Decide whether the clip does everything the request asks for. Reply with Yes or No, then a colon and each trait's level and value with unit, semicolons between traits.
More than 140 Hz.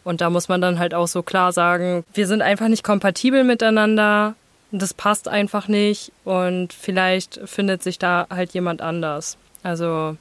Yes: medium, 185 Hz